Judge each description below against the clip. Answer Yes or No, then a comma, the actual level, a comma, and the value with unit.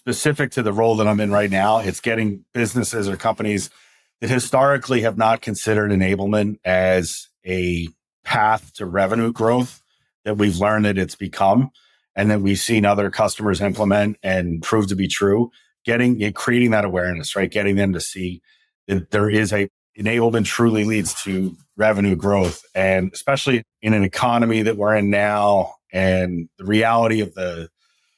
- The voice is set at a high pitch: No, low, 105 Hz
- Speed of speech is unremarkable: Yes, average, 165 wpm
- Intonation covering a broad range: No, average, 2.8 semitones